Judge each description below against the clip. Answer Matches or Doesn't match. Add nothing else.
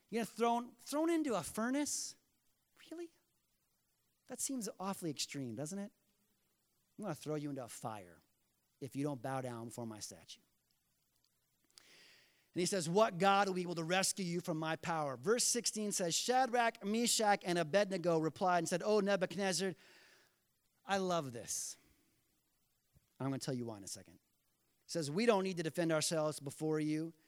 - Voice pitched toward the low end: Doesn't match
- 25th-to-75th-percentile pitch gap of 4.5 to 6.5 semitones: Matches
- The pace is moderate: Matches